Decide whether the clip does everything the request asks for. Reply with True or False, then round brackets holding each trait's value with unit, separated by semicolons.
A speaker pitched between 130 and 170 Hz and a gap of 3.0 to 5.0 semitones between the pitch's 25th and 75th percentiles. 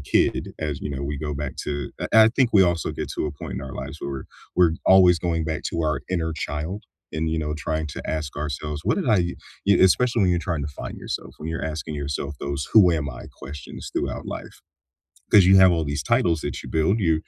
False (80 Hz; 3.4 semitones)